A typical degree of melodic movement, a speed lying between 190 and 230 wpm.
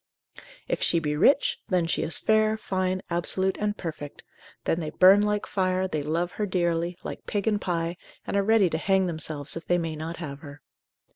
Yes: average, 3.1 semitones; average, 200 wpm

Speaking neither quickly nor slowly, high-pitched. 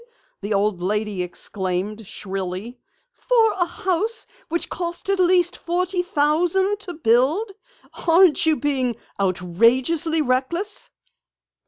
No: slow, 110 wpm; very high, 300 Hz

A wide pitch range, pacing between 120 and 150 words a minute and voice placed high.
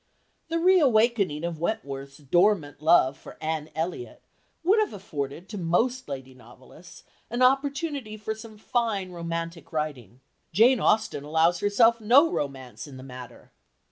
No: wide, 7.8 semitones; average, 140 wpm; medium, 175 Hz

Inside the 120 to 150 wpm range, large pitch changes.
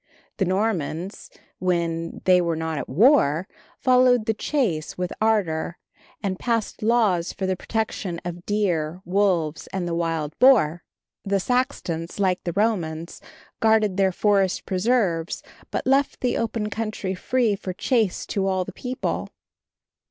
No: average, 140 wpm; average, 4.5 semitones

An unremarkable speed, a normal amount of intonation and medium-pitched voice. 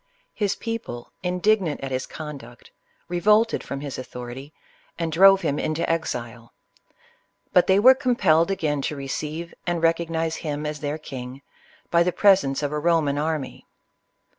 Yes: average, 155 wpm; average, 4.2 semitones; medium, 160 Hz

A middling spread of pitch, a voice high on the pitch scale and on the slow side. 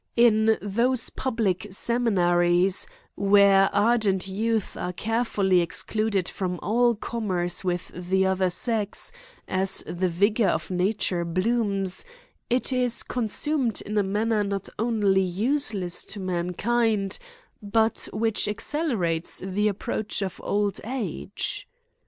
Yes: average, 3.3 semitones; high, 205 Hz; slow, 120 wpm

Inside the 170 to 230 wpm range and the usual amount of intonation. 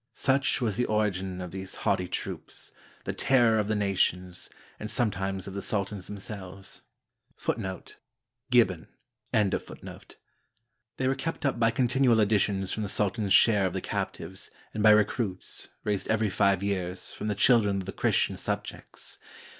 No: average, 155 wpm; average, 3.2 semitones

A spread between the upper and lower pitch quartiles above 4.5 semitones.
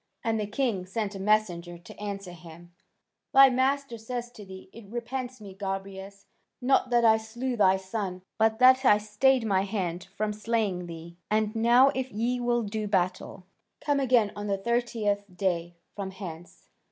No: average, 3.9 semitones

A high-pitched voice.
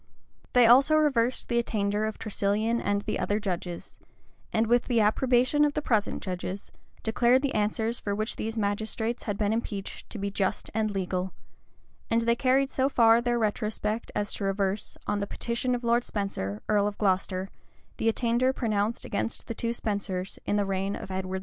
Yes: high, 215 Hz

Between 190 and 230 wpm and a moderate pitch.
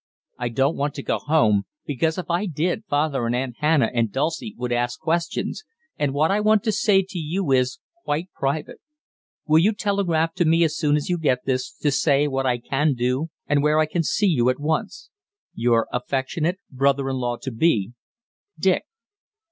Yes: average, 195 wpm; medium, 145 Hz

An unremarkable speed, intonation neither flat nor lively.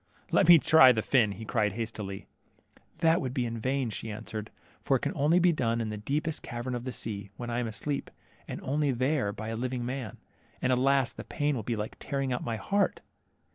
No: fast, 220 wpm; average, 3.7 semitones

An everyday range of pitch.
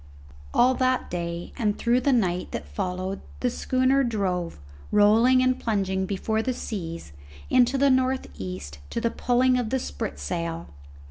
No: wide, 6.3 semitones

